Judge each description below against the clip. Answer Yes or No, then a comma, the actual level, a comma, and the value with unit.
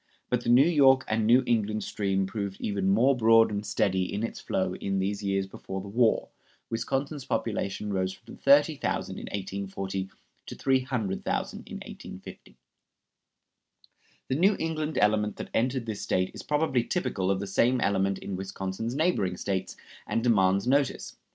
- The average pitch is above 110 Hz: No, low, 105 Hz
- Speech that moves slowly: No, average, 155 wpm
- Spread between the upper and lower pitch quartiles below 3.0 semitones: No, average, 4.8 semitones